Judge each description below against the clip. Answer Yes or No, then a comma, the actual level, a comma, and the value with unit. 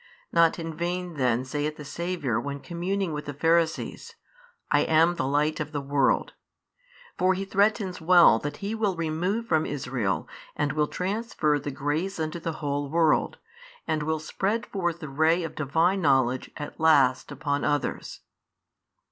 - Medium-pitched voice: Yes, medium, 160 Hz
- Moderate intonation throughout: Yes, average, 3.5 semitones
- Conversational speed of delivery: Yes, average, 160 wpm